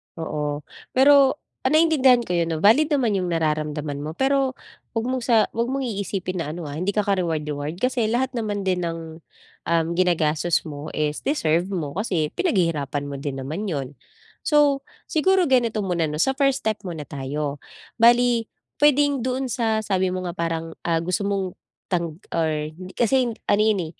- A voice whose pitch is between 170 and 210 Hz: Yes, medium, 185 Hz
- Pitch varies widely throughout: Yes, wide, 7.5 semitones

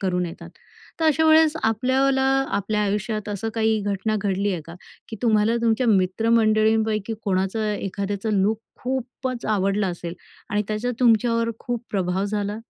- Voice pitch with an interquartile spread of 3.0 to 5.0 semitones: No, narrow, 2.6 semitones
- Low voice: No, high, 215 Hz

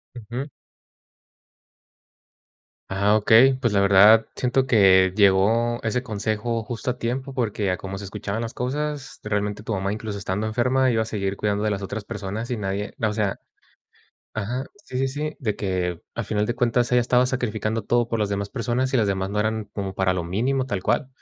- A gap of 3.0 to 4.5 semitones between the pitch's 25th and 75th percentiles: Yes, average, 3.3 semitones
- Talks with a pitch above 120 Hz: No, low, 110 Hz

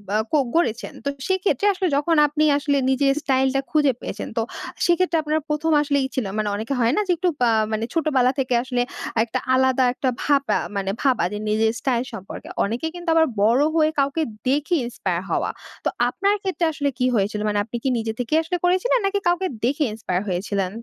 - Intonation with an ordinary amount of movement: No, wide, 6.0 semitones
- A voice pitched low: No, very high, 275 Hz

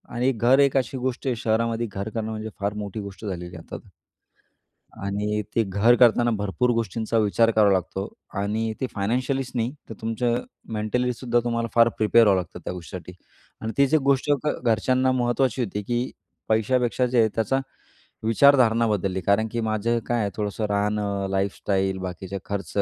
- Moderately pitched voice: No, low, 110 Hz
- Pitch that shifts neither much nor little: Yes, average, 3.1 semitones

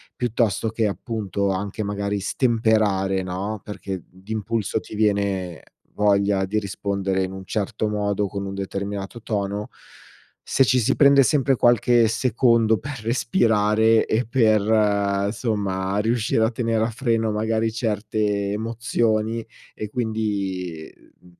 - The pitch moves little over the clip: Yes, narrow, 2.3 semitones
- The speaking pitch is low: Yes, low, 105 Hz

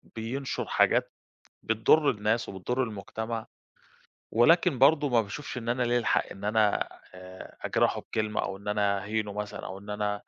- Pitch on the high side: No, low, 110 Hz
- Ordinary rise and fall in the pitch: Yes, average, 3.0 semitones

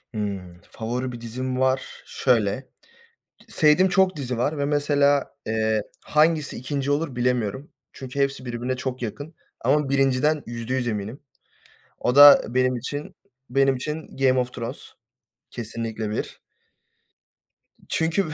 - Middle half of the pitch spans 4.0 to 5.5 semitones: No, average, 3.4 semitones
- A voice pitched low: Yes, low, 130 Hz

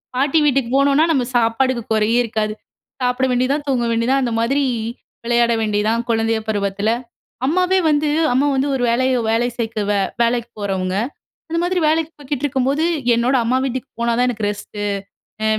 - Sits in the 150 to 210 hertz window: No, high, 245 Hz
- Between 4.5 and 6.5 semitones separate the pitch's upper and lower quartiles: No, average, 3.4 semitones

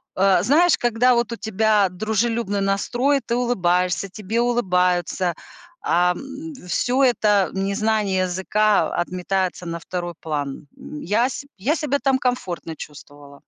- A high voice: Yes, high, 200 Hz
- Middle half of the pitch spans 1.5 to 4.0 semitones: No, average, 5.0 semitones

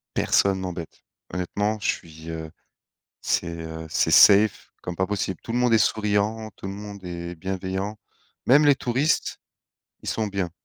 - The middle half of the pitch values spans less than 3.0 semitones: No, average, 3.7 semitones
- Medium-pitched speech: No, low, 100 Hz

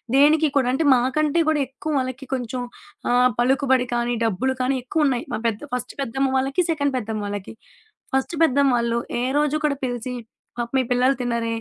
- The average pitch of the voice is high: Yes, very high, 260 Hz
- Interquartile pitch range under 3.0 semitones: Yes, narrow, 2.4 semitones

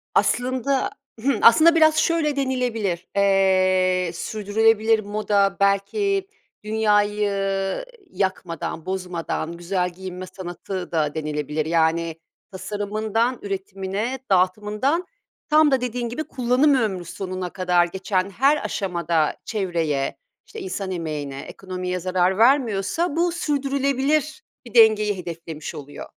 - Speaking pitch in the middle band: No, high, 200 Hz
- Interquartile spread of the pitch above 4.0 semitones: Yes, wide, 5.6 semitones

